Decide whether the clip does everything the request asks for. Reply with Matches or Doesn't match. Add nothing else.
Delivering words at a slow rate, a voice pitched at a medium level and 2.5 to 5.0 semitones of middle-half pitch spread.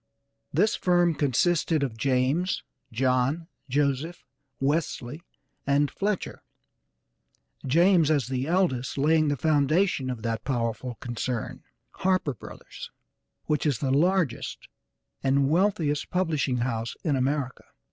Matches